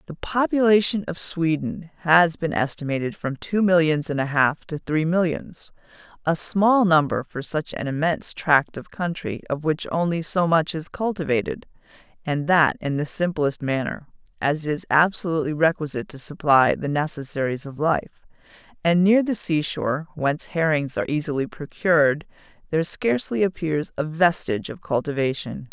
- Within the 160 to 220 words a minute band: No, average, 145 wpm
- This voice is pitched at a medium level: Yes, medium, 160 Hz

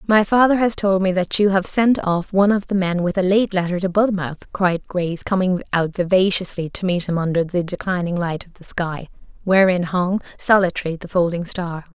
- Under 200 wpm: No, fast, 205 wpm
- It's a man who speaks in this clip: No, female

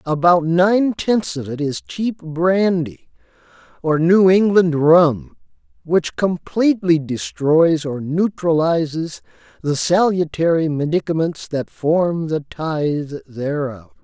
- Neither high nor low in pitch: Yes, medium, 165 Hz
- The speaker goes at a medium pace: No, slow, 105 wpm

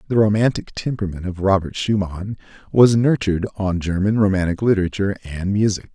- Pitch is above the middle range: No, low, 100 Hz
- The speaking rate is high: No, average, 140 wpm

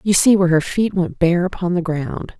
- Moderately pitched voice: Yes, medium, 180 Hz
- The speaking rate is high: Yes, fast, 250 wpm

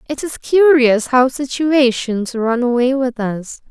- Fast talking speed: No, average, 145 wpm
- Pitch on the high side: Yes, very high, 255 Hz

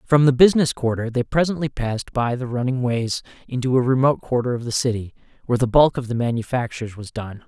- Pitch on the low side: Yes, low, 125 Hz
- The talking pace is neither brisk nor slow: No, fast, 210 wpm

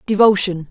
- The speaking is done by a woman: Yes, female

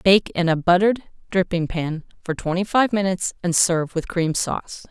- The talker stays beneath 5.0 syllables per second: No, 5.4 syllables/s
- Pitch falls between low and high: Yes, medium, 180 Hz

